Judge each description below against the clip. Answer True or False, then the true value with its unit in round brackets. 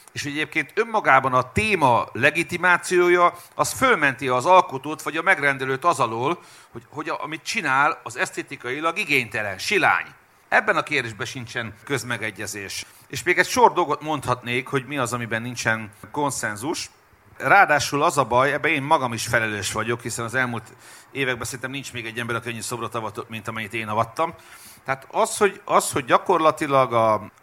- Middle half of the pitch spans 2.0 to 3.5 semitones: False (4.9 semitones)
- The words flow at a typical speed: False (165 wpm)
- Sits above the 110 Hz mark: True (130 Hz)